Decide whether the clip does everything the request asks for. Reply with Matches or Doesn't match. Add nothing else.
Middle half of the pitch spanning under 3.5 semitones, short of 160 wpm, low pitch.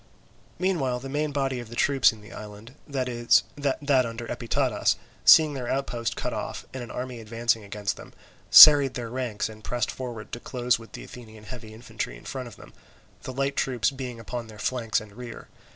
Doesn't match